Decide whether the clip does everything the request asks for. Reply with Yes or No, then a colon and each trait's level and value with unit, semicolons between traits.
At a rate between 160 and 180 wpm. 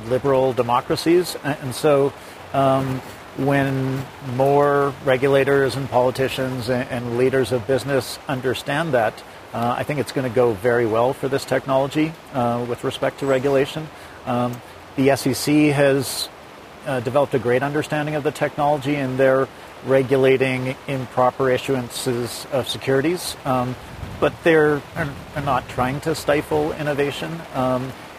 No: slow, 135 wpm